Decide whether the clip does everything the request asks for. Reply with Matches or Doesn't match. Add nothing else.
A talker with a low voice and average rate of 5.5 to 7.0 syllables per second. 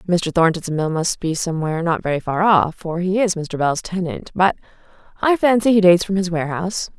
Doesn't match